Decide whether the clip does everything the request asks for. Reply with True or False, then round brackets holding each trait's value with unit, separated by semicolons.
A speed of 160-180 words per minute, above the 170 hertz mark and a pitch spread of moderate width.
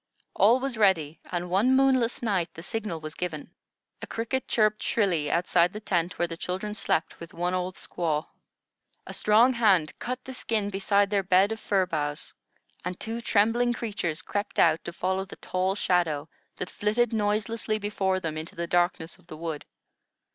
True (175 wpm; 190 Hz; 4.1 semitones)